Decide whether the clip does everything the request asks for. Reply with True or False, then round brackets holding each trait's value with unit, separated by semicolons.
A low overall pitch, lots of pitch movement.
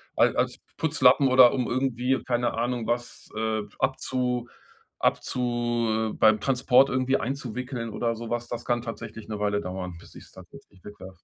False (120 Hz; 2.4 semitones)